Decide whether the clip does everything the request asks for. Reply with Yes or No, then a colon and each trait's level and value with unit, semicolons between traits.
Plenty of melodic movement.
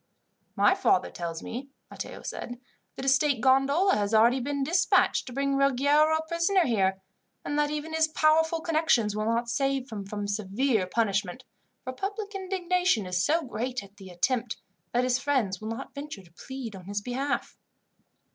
Yes: wide, 6.0 semitones